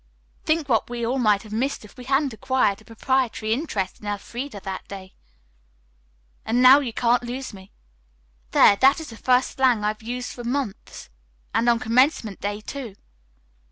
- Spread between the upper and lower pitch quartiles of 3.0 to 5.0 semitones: Yes, average, 3.7 semitones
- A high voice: Yes, high, 240 Hz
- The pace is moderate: Yes, average, 170 wpm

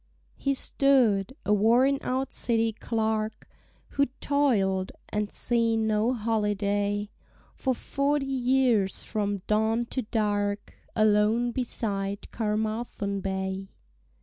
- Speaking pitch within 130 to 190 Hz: No, high, 220 Hz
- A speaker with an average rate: No, slow, 100 wpm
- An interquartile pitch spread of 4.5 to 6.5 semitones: No, average, 3.0 semitones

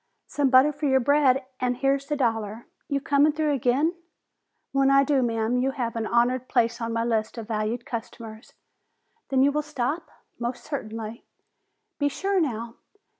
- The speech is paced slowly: No, average, 170 wpm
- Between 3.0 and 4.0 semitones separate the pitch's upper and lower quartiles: Yes, average, 3.5 semitones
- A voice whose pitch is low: No, very high, 255 Hz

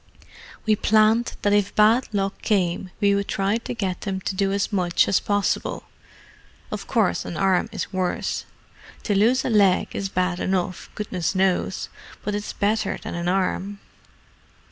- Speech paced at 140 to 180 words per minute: Yes, average, 160 wpm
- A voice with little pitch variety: Yes, narrow, 2.0 semitones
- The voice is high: Yes, high, 200 Hz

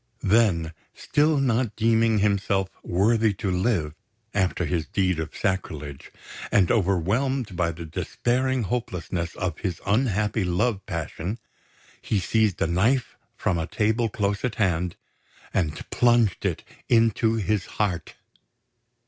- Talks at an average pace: No, slow, 125 wpm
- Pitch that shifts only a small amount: No, average, 4.3 semitones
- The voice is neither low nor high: No, low, 100 Hz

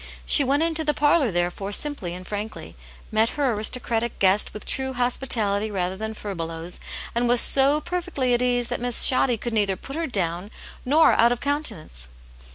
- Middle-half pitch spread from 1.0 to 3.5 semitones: No, average, 5.2 semitones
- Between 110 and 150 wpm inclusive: No, average, 175 wpm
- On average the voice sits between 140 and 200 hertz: No, high, 235 Hz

